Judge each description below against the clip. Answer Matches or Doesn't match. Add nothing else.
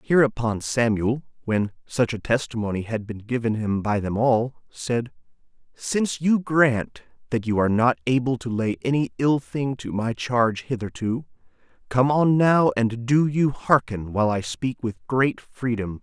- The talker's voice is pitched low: Matches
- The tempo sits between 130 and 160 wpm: Doesn't match